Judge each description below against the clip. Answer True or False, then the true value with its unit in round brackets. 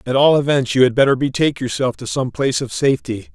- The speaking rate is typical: False (235 wpm)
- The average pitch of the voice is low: True (130 Hz)